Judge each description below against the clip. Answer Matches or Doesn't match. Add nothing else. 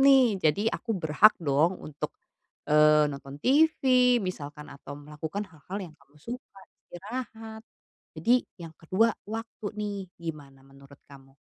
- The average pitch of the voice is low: Doesn't match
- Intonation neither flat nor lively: Doesn't match